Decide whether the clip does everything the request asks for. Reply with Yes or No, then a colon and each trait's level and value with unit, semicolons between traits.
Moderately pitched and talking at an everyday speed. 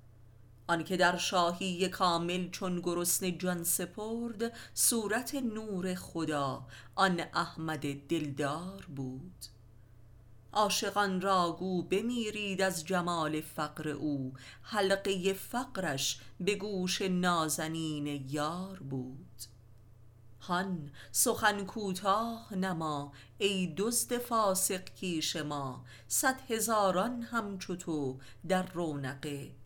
No: medium, 175 Hz; slow, 90 wpm